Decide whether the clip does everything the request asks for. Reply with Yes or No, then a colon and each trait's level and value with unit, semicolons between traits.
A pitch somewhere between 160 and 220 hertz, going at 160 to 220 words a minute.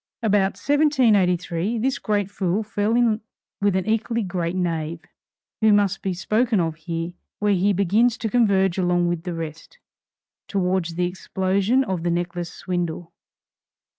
No: high, 190 Hz; average, 145 wpm